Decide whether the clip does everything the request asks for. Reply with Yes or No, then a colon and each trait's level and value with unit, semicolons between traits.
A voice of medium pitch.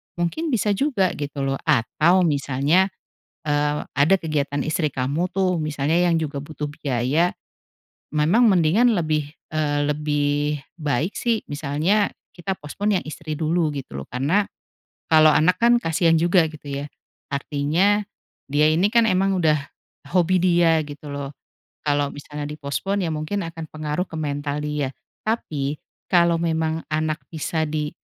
Yes: medium, 155 Hz